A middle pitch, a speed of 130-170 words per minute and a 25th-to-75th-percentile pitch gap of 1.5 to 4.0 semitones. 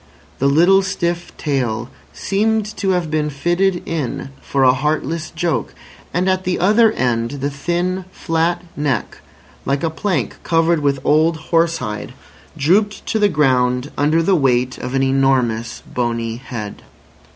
No: medium, 155 Hz; average, 150 wpm; average, 5.0 semitones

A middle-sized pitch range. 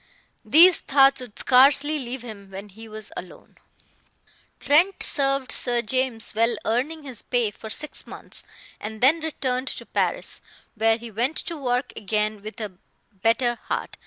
Yes: average, 4.0 semitones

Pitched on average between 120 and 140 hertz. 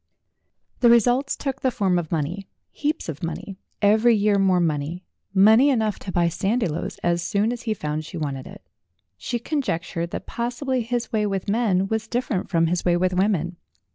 No: high, 200 Hz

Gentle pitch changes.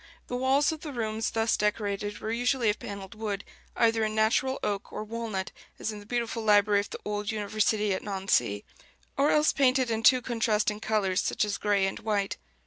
Yes: narrow, 2.1 semitones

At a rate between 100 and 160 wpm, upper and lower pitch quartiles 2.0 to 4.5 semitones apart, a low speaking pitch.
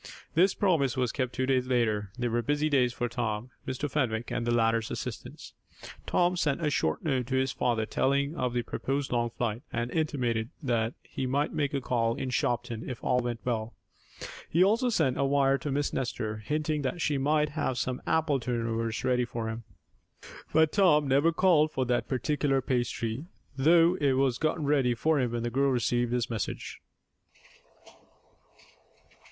No: average, 180 wpm; average, 3.7 semitones; low, 130 Hz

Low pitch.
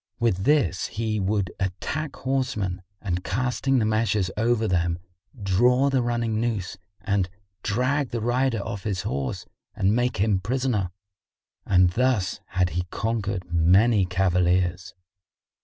Yes: low, 105 Hz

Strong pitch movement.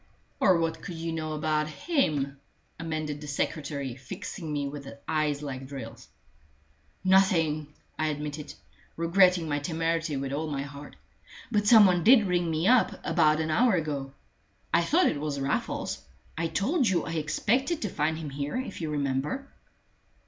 No: average, 3.4 semitones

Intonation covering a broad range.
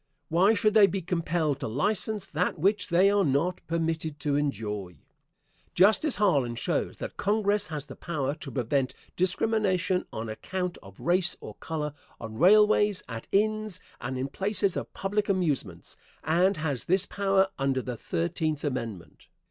Yes: wide, 6.4 semitones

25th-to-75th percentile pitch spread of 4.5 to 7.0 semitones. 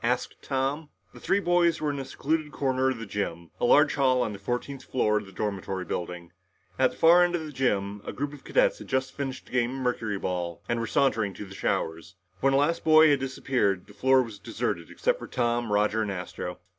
Yes: wide, 5.6 semitones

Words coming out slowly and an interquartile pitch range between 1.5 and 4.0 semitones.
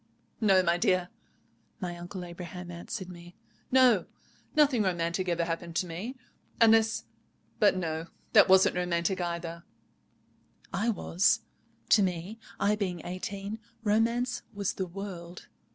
Yes: slow, 115 wpm; average, 3.3 semitones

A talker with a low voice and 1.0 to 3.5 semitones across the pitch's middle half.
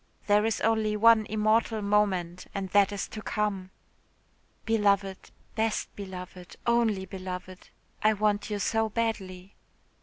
No: high, 205 Hz; narrow, 2.4 semitones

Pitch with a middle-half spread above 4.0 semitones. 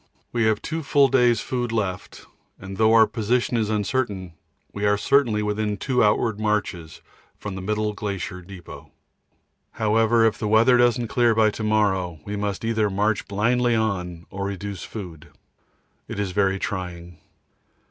No: average, 2.7 semitones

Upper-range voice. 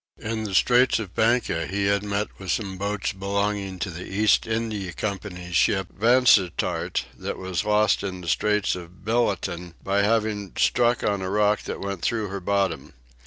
No: low, 100 Hz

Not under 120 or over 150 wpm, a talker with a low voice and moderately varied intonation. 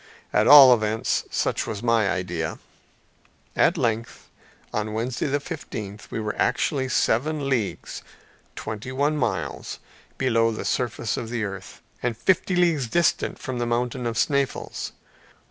Yes: average, 140 wpm; low, 120 Hz; average, 4.0 semitones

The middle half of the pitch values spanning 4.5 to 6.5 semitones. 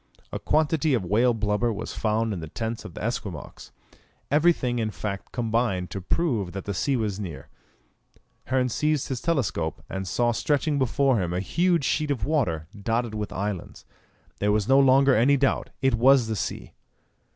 Yes: average, 5.1 semitones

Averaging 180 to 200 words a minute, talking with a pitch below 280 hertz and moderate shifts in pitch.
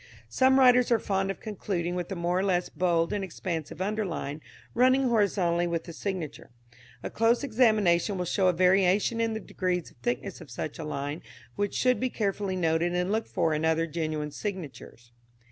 Yes: average, 185 wpm; medium, 185 Hz; average, 4.2 semitones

